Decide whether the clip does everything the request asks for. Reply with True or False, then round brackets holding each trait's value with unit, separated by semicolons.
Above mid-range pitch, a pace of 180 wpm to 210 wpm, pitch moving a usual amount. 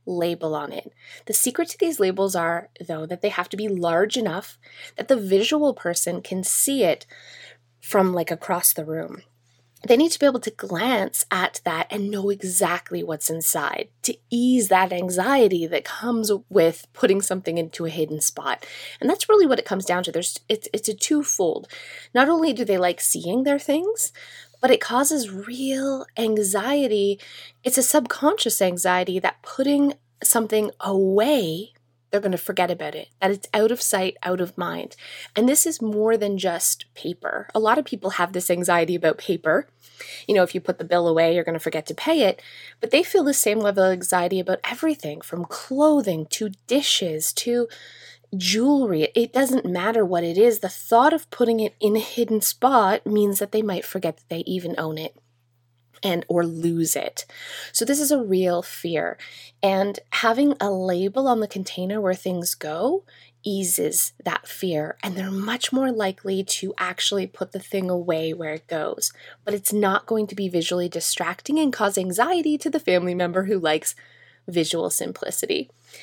False (195 Hz; 185 wpm; 5.7 semitones)